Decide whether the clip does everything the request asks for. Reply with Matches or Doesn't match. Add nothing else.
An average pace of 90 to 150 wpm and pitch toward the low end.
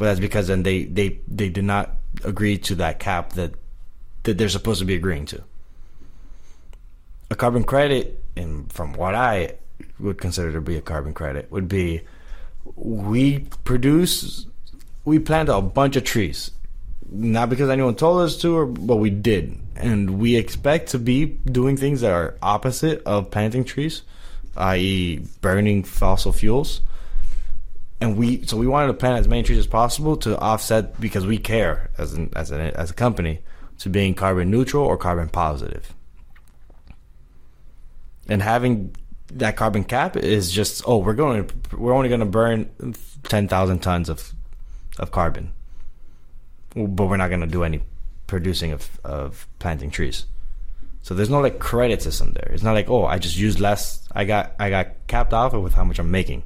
Doesn't match